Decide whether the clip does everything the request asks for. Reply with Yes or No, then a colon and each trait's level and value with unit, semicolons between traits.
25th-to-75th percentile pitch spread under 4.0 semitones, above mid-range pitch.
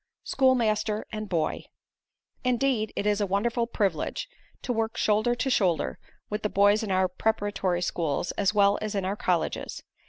Yes: average, 2.8 semitones; high, 210 Hz